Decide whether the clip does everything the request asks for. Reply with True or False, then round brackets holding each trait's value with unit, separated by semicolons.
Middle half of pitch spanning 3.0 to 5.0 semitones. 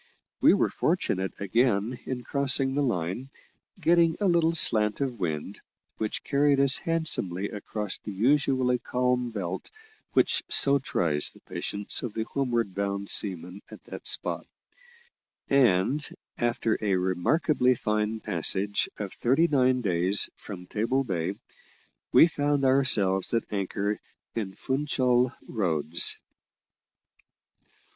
False (5.6 semitones)